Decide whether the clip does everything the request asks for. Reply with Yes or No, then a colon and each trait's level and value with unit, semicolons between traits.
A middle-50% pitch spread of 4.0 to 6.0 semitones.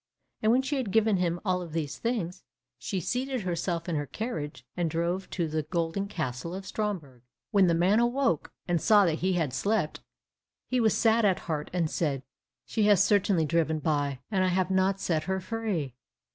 Yes: average, 4.5 semitones